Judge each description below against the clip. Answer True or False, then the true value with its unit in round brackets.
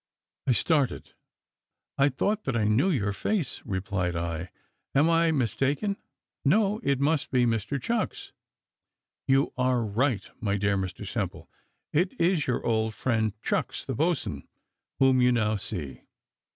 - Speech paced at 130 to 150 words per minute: True (140 wpm)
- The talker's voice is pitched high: False (125 Hz)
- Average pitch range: False (6.2 semitones)